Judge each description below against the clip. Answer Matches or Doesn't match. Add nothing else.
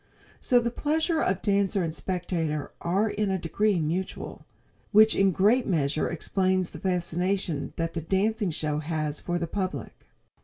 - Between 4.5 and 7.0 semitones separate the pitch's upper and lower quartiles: Doesn't match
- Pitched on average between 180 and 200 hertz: Matches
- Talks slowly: Doesn't match